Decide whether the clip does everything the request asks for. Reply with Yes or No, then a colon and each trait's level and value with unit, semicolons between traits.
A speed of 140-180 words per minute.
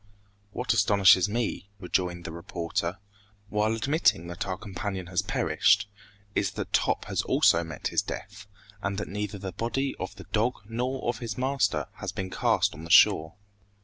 Yes: average, 170 wpm